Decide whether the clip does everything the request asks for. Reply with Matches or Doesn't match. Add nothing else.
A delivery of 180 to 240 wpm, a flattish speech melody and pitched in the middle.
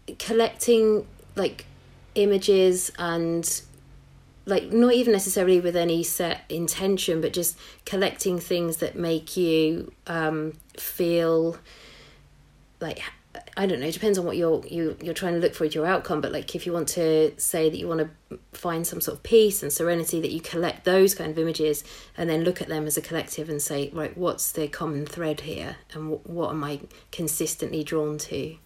Matches